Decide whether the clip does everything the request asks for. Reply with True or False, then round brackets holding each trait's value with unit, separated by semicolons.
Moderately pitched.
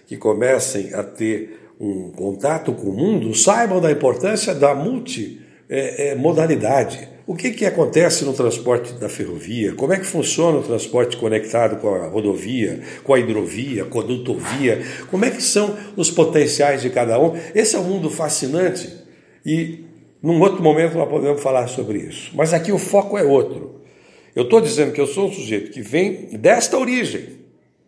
True (155 Hz)